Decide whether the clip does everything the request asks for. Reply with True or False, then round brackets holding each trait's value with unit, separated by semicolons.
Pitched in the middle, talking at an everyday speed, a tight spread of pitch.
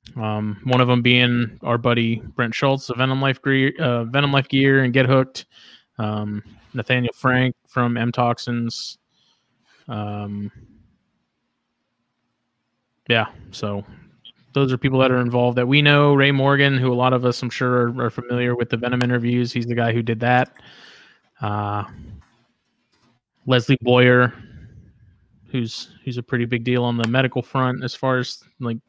False (125 Hz; 160 wpm; 1.8 semitones)